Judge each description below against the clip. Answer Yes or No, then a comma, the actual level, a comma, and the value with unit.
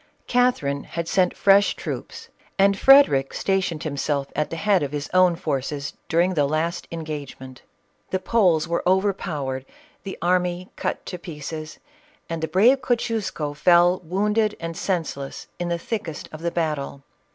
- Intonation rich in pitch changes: No, average, 4.2 semitones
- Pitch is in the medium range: Yes, medium, 170 Hz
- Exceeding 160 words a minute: No, average, 150 wpm